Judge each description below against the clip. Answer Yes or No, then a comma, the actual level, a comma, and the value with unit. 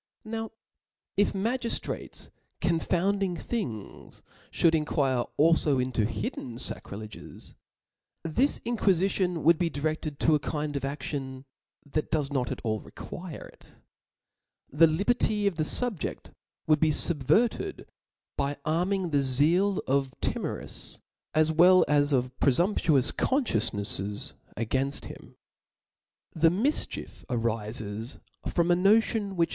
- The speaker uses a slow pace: Yes, slow, 120 wpm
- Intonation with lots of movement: Yes, wide, 6.0 semitones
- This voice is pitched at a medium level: Yes, medium, 155 Hz